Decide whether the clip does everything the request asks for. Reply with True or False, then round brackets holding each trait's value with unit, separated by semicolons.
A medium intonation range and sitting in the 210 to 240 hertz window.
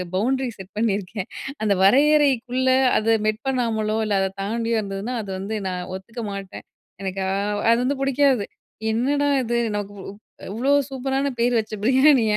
True (4.4 semitones; 230 Hz)